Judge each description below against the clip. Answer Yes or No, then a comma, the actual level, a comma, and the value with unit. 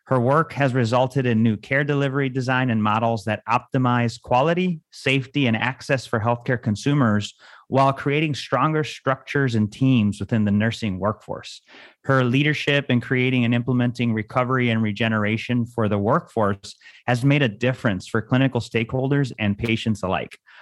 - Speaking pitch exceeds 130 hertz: No, low, 125 Hz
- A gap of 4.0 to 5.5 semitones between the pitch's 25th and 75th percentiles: No, average, 3.4 semitones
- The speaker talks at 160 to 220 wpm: No, average, 150 wpm